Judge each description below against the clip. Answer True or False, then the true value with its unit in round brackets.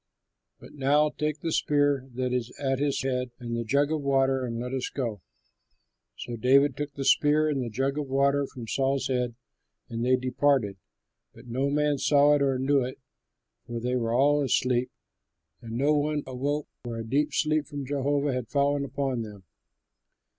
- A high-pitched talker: False (135 Hz)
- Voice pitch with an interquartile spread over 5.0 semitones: False (2.5 semitones)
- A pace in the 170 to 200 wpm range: True (180 wpm)